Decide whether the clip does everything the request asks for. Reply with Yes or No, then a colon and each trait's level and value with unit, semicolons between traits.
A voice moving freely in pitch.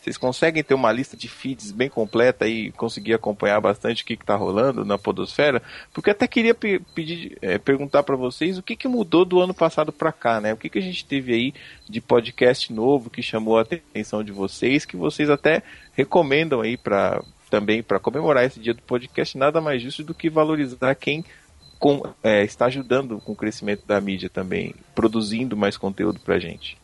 Yes: wide, 5.8 semitones